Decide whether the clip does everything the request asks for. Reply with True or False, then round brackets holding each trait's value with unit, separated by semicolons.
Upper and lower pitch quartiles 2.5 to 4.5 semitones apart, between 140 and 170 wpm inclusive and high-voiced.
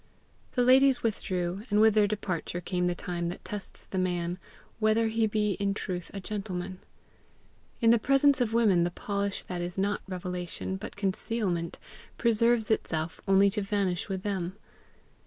True (3.4 semitones; 160 wpm; 200 Hz)